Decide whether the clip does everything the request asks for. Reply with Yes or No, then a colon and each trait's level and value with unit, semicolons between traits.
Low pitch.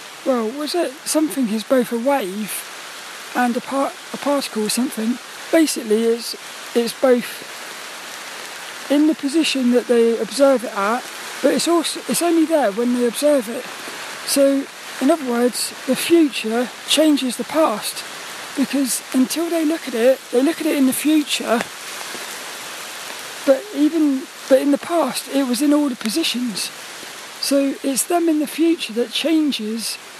No: very high, 270 Hz